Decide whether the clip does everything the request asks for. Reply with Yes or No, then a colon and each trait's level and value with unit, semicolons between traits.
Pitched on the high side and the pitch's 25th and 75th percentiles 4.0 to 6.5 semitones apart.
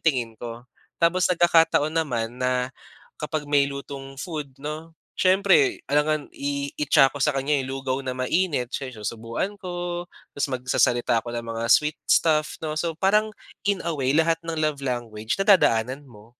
No: medium, 145 Hz; average, 4.4 semitones